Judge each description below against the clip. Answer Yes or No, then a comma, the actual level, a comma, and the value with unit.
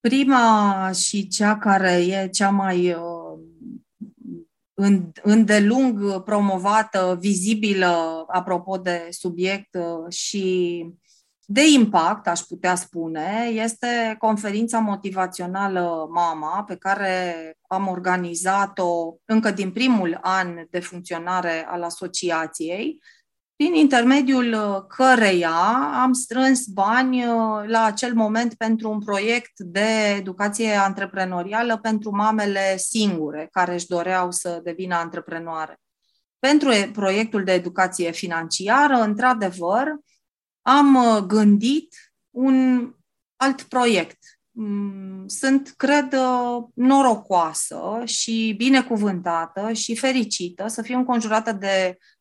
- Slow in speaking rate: Yes, slow, 95 wpm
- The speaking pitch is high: Yes, high, 200 Hz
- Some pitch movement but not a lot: Yes, average, 4.1 semitones